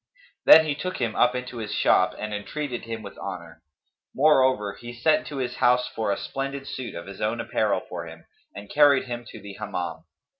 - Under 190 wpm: No, average, 200 wpm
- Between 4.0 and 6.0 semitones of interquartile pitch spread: Yes, average, 4.5 semitones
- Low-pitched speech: Yes, low, 120 Hz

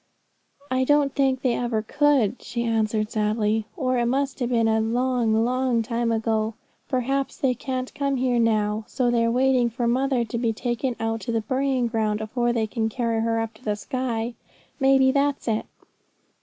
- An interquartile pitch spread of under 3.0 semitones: Yes, narrow, 2.6 semitones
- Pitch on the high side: Yes, high, 240 Hz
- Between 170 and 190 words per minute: Yes, average, 185 wpm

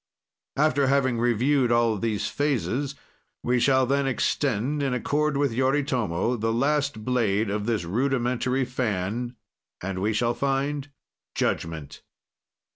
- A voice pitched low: Yes, low, 125 Hz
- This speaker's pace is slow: Yes, slow, 120 wpm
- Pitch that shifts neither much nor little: Yes, average, 3.5 semitones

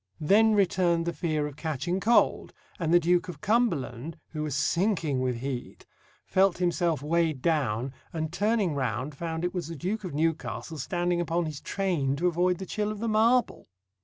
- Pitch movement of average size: Yes, average, 3.8 semitones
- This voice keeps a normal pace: Yes, average, 180 wpm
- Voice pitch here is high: No, medium, 170 Hz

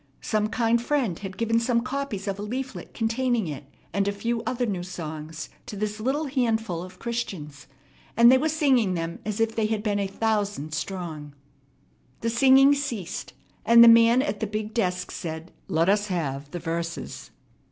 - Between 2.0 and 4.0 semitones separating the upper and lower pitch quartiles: No, average, 4.7 semitones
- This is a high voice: Yes, high, 215 Hz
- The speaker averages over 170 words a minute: Yes, average, 180 wpm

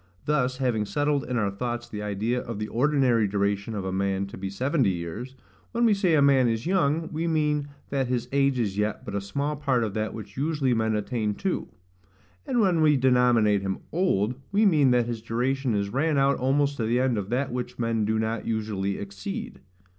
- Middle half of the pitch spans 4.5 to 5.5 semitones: Yes, average, 5.1 semitones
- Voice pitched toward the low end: Yes, low, 125 Hz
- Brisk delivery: Yes, fast, 210 wpm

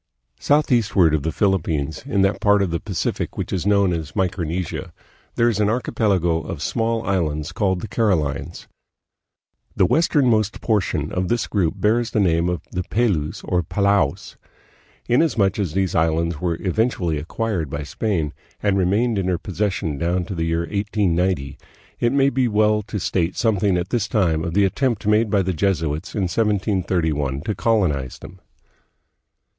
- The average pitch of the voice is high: No, very low, 95 Hz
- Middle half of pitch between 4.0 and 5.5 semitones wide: Yes, average, 4.4 semitones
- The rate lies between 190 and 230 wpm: No, average, 165 wpm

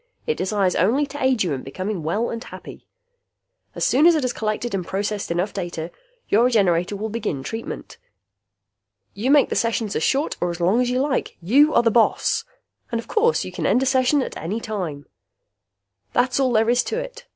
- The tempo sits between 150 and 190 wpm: No, fast, 205 wpm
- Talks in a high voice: Yes, high, 225 Hz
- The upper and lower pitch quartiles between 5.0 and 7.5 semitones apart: Yes, wide, 5.4 semitones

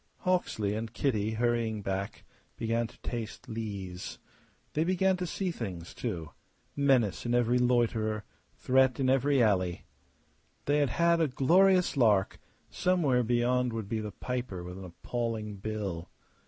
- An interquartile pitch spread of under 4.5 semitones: Yes, average, 4.0 semitones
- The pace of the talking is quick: No, average, 140 wpm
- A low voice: Yes, low, 115 Hz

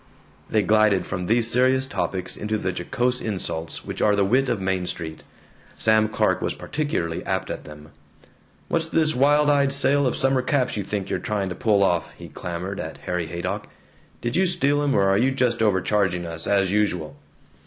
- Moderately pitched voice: No, low, 105 Hz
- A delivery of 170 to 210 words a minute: Yes, average, 190 wpm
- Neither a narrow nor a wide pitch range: No, wide, 6.1 semitones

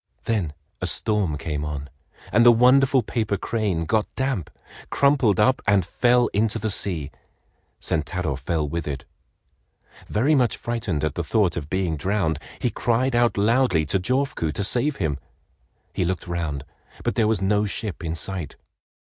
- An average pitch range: No, wide, 6.4 semitones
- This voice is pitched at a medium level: No, low, 100 Hz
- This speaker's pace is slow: No, average, 160 wpm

